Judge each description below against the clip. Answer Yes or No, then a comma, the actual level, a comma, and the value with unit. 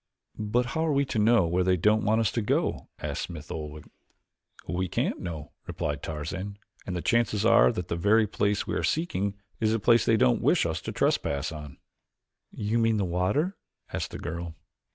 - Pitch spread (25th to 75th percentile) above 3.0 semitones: Yes, average, 4.9 semitones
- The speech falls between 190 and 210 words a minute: Yes, average, 195 wpm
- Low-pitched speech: Yes, low, 100 Hz